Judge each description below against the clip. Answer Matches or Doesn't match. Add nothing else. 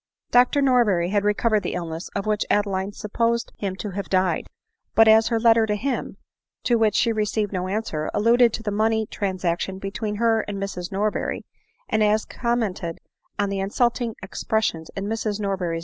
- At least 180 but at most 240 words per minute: Matches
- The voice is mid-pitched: Doesn't match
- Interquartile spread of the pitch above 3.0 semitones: Doesn't match